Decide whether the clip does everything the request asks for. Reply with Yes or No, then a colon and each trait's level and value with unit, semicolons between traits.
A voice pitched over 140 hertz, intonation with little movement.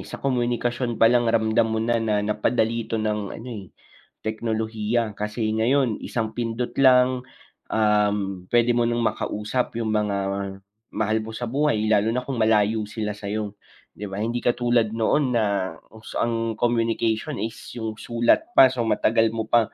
No: low, 115 Hz; narrow, 1.8 semitones